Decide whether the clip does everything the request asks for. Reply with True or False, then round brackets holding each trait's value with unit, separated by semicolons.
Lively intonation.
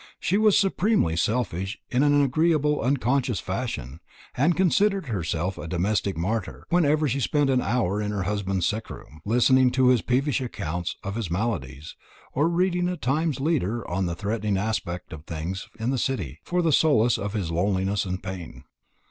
True (7.4 semitones)